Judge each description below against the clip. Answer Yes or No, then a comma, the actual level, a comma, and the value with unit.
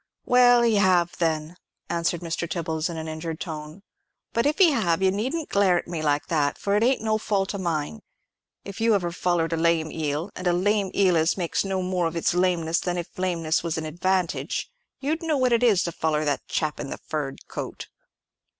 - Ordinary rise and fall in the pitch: Yes, average, 3.9 semitones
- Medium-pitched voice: Yes, medium, 175 Hz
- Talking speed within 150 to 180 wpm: No, fast, 205 wpm